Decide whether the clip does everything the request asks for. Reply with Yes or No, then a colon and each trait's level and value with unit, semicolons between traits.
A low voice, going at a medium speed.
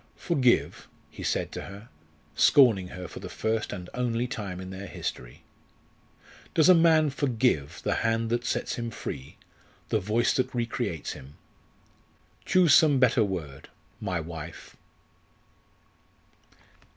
No: low, 115 Hz; slow, 130 wpm